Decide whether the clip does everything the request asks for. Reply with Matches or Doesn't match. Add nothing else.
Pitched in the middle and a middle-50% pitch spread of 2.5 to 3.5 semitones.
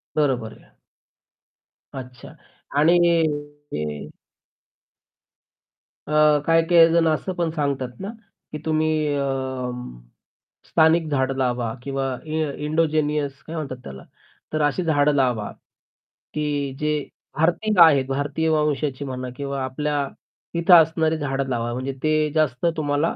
Matches